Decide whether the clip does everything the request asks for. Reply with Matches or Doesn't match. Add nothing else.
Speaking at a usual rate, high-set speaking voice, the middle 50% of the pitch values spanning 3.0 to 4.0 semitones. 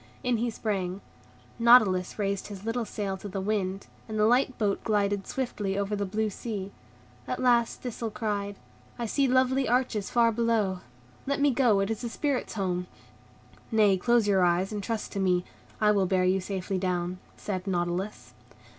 Matches